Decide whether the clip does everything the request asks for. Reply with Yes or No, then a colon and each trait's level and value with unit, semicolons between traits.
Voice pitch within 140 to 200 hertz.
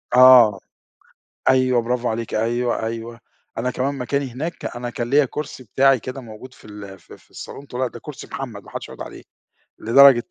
No: low, 125 Hz